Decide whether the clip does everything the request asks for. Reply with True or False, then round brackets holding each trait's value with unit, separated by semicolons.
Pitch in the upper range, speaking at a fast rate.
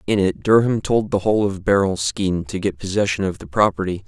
False (100 Hz; 220 wpm)